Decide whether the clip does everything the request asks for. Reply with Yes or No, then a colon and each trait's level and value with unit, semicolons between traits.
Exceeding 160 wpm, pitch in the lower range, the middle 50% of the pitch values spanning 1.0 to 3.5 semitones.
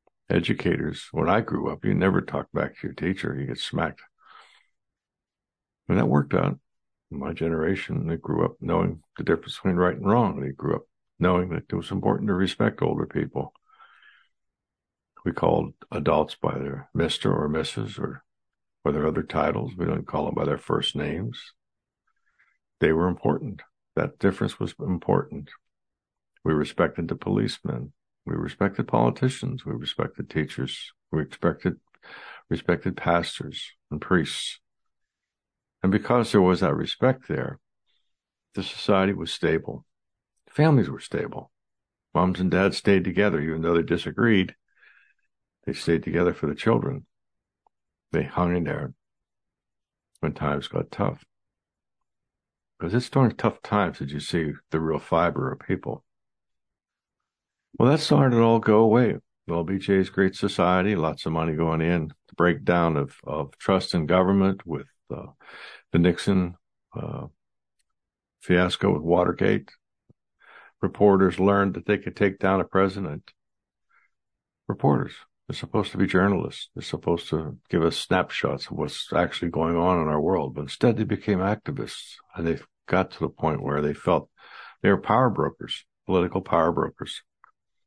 No: average, 150 wpm; very low, 90 Hz; average, 3.2 semitones